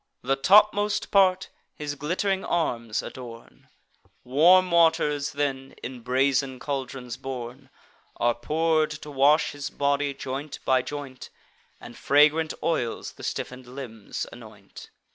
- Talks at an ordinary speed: No, slow, 120 wpm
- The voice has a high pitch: No, medium, 140 Hz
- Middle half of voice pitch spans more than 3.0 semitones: Yes, average, 3.5 semitones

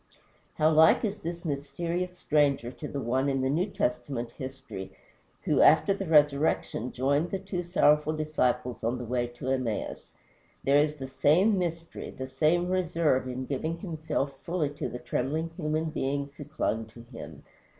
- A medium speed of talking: Yes, average, 165 wpm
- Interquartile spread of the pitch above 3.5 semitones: Yes, average, 4.1 semitones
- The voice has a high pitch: No, medium, 145 Hz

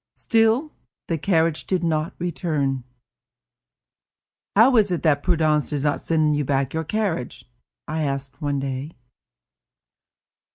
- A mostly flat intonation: No, average, 3.8 semitones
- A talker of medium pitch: Yes, medium, 155 Hz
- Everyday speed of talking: No, slow, 125 wpm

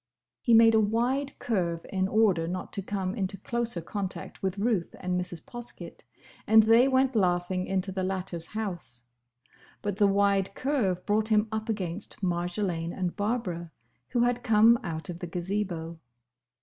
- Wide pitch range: No, average, 3.8 semitones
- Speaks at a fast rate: No, average, 160 wpm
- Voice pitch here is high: Yes, high, 195 Hz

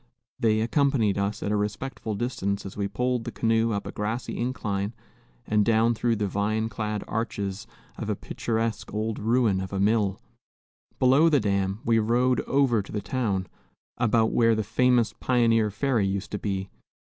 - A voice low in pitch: Yes, low, 110 Hz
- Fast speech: No, average, 170 wpm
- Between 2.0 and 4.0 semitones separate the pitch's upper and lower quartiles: Yes, narrow, 2.6 semitones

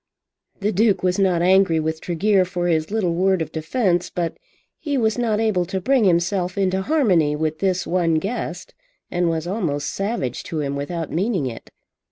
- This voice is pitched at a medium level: Yes, medium, 180 Hz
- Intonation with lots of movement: No, average, 3.5 semitones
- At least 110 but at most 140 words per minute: No, average, 180 wpm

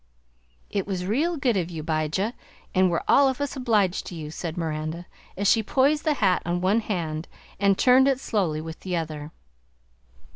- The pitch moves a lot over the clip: Yes, wide, 6.5 semitones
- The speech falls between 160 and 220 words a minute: Yes, average, 185 wpm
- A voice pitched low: No, medium, 185 Hz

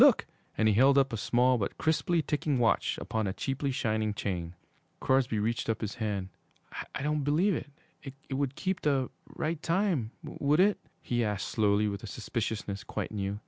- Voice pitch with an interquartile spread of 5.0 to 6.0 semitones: Yes, wide, 5.5 semitones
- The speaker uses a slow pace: No, average, 180 wpm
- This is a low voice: Yes, low, 125 Hz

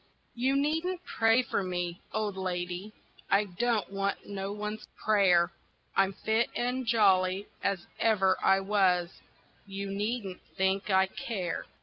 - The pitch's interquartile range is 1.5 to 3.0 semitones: Yes, average, 2.7 semitones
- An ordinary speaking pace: No, slow, 130 wpm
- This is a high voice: Yes, high, 200 Hz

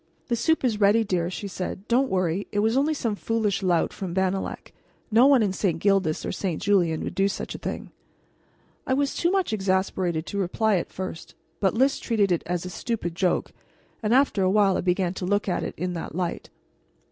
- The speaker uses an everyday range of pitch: Yes, average, 3.7 semitones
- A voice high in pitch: Yes, high, 195 Hz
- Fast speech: Yes, fast, 210 wpm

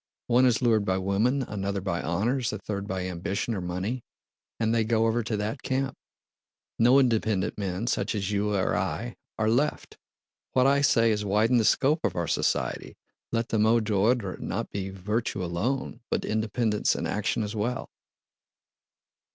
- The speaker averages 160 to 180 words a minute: Yes, average, 170 wpm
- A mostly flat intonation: No, average, 3.4 semitones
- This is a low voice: Yes, low, 110 Hz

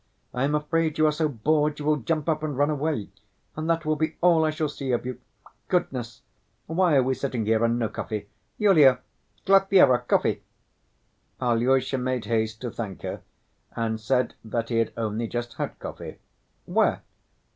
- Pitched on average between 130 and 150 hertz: Yes, low, 135 Hz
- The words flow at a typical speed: Yes, average, 180 wpm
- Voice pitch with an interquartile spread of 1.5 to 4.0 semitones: No, average, 4.9 semitones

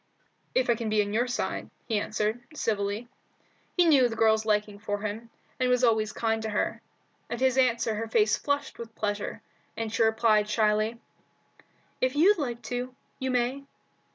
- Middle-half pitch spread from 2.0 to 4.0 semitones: Yes, narrow, 2.6 semitones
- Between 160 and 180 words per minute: Yes, average, 175 wpm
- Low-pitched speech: No, high, 225 Hz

